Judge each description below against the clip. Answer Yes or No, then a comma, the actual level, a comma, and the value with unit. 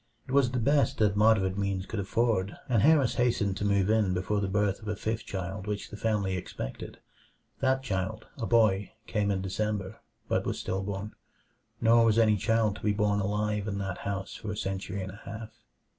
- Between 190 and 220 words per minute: Yes, fast, 205 wpm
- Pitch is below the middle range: Yes, low, 105 Hz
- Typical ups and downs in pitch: No, narrow, 2.3 semitones